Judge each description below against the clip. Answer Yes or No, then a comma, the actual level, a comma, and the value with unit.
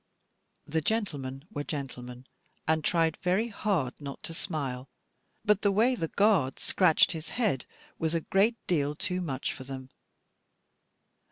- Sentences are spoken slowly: No, average, 145 wpm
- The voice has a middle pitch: Yes, medium, 160 Hz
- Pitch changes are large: Yes, wide, 6.2 semitones